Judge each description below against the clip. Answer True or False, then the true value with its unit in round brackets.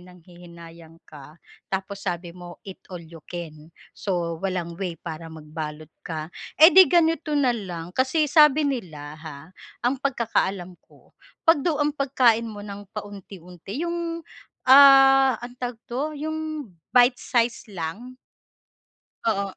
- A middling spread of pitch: False (7.4 semitones)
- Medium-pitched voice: False (200 Hz)